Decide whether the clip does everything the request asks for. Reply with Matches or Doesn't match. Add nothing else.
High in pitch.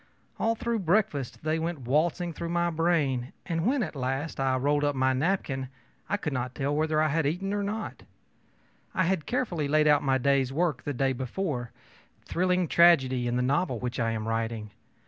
Doesn't match